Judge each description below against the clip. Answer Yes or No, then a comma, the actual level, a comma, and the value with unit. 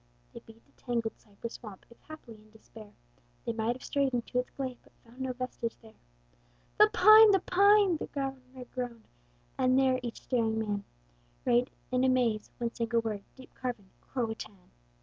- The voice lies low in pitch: No, high, 245 Hz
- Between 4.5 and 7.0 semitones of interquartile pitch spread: No, average, 2.7 semitones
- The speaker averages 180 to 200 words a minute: Yes, average, 185 wpm